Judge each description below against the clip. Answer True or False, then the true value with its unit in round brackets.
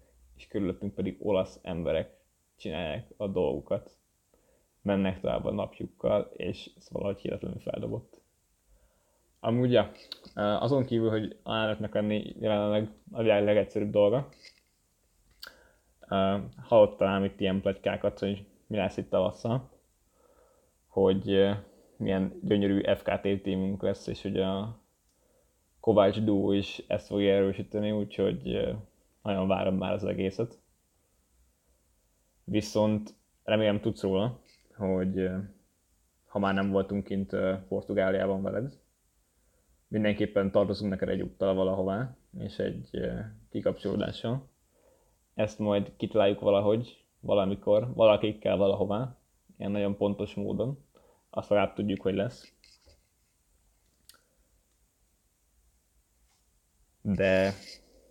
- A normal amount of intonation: False (1.7 semitones)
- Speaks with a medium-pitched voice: False (100 Hz)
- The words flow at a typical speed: False (100 wpm)